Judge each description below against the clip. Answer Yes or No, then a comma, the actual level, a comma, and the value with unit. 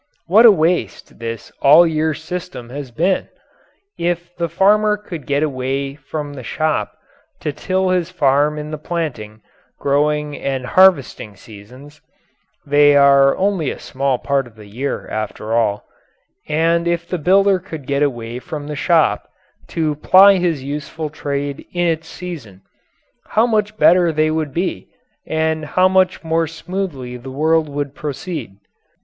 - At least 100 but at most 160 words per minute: Yes, average, 150 wpm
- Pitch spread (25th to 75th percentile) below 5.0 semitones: Yes, average, 4.0 semitones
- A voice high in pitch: No, medium, 155 Hz